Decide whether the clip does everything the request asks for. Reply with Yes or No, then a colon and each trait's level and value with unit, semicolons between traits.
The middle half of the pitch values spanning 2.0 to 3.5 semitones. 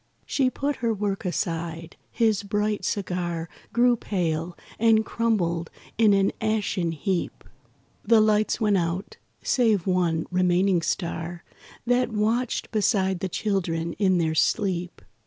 No: average, 4.1 semitones